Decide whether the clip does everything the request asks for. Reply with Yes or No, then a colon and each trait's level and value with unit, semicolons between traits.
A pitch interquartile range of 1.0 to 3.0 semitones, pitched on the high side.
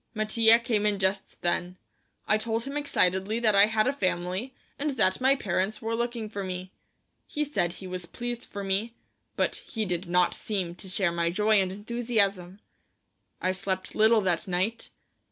No: average, 3.6 semitones; high, 205 Hz